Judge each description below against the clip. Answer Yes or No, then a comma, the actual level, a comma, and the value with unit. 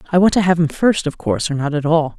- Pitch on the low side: No, medium, 160 Hz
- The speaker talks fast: Yes, fast, 330 wpm